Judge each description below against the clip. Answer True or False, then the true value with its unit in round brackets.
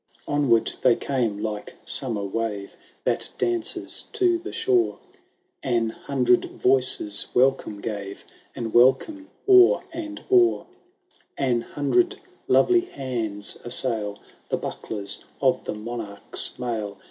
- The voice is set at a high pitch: False (125 Hz)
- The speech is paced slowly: True (110 wpm)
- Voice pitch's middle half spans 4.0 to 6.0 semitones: True (5.3 semitones)